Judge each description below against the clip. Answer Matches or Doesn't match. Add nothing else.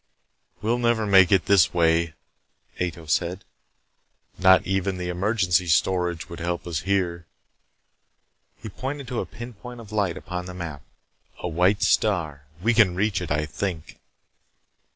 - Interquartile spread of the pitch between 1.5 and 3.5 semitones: Matches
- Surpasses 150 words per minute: Doesn't match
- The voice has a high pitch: Doesn't match